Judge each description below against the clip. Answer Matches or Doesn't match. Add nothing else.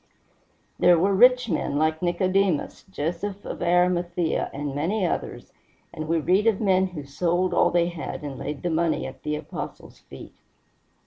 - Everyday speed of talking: Matches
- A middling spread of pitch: Matches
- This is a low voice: Doesn't match